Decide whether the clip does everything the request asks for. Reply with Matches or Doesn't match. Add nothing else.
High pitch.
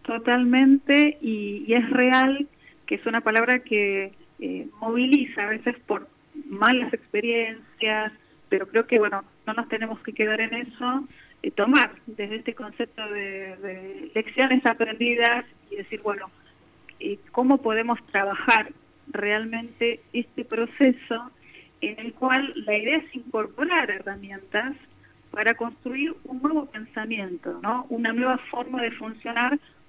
Matches